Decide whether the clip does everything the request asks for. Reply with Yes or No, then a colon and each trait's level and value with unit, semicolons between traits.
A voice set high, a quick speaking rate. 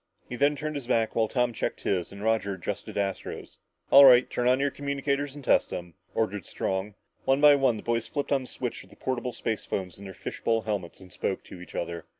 No: low, 115 Hz; fast, 230 wpm